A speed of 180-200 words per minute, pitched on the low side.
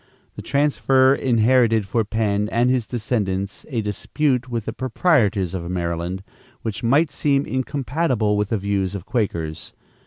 No: average, 145 wpm; low, 115 Hz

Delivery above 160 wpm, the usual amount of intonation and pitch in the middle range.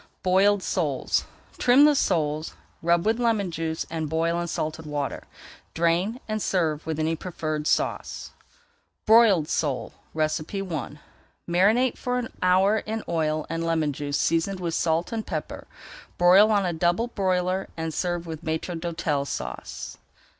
No: average, 145 wpm; average, 3.6 semitones; medium, 170 Hz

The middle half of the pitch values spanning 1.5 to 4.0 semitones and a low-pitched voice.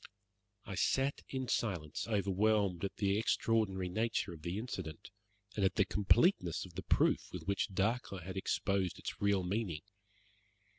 Yes: average, 3.1 semitones; low, 100 Hz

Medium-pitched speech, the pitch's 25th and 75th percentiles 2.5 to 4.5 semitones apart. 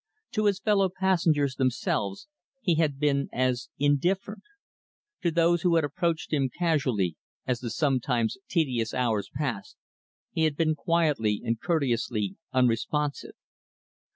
No: medium, 145 Hz; average, 5.3 semitones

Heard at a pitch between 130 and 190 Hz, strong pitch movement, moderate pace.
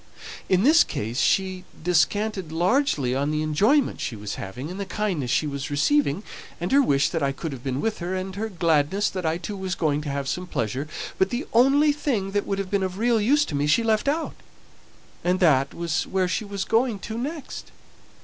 No: medium, 185 Hz; wide, 6.6 semitones; fast, 215 wpm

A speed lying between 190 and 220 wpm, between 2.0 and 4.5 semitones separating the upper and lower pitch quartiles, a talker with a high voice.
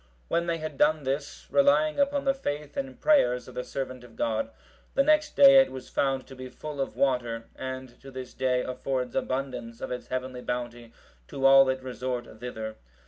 No: average, 195 wpm; average, 3.5 semitones; low, 130 Hz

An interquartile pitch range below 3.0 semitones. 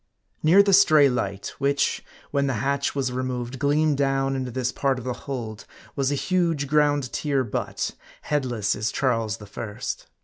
Yes: narrow, 2.6 semitones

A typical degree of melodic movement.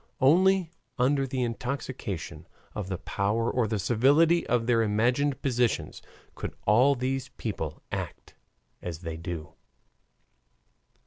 Yes: average, 4.6 semitones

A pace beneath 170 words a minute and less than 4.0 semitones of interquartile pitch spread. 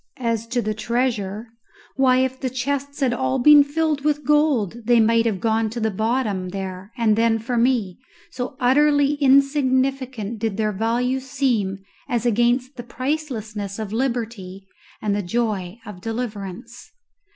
Yes: average, 150 wpm; average, 3.5 semitones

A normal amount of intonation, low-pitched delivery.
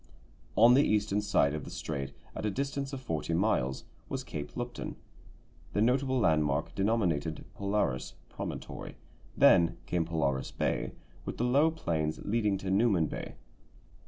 No: wide, 7.2 semitones; low, 100 Hz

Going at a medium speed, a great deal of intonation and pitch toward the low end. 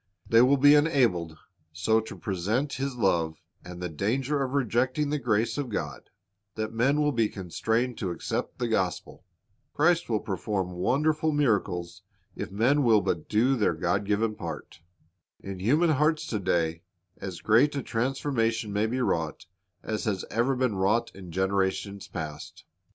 Yes: average, 160 wpm; wide, 5.8 semitones; low, 110 Hz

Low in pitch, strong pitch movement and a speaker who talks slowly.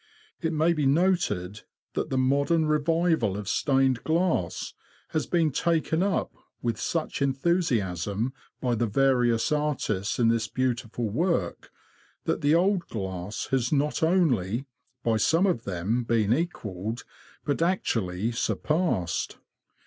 Yes: low, 130 Hz; wide, 6.8 semitones; slow, 125 wpm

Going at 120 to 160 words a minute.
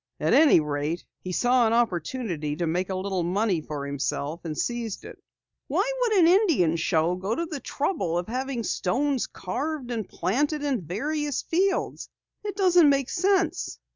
No: average, 170 wpm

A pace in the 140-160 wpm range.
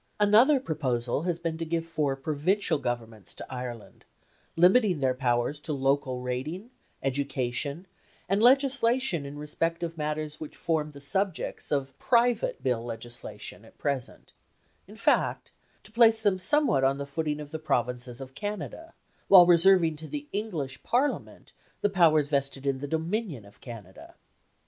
Yes: average, 150 wpm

